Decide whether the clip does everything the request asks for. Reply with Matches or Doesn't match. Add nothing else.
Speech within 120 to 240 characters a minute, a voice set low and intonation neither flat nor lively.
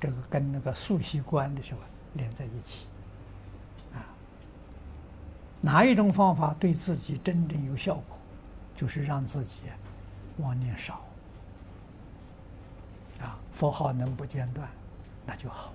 Doesn't match